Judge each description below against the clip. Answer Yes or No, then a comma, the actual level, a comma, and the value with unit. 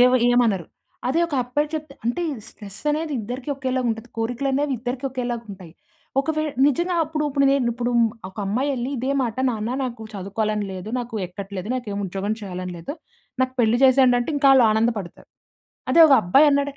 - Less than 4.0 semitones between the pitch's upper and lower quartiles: No, average, 4.4 semitones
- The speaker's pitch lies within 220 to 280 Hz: Yes, high, 245 Hz